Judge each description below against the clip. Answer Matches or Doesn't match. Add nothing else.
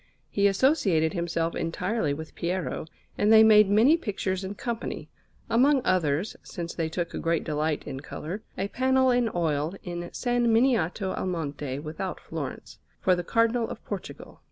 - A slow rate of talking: Doesn't match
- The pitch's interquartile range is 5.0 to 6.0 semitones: Matches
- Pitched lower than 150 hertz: Doesn't match